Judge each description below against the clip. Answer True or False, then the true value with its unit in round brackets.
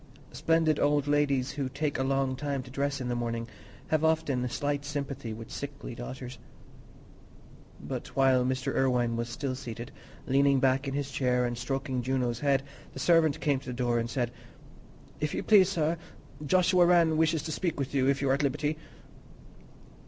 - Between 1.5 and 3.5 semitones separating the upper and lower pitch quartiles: True (2.6 semitones)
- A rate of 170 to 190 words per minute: True (180 wpm)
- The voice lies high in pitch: False (135 Hz)